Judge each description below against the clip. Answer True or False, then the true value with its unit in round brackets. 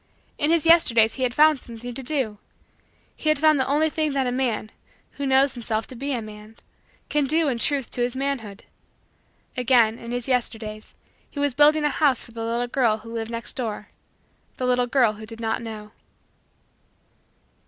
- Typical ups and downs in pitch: True (3.7 semitones)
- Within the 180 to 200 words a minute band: True (190 wpm)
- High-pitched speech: True (245 Hz)